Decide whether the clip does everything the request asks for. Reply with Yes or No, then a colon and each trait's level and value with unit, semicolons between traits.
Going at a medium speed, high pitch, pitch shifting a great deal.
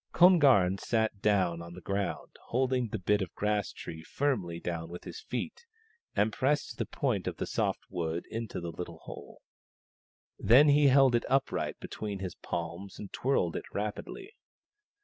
No: average, 170 wpm; low, 105 Hz; wide, 7.0 semitones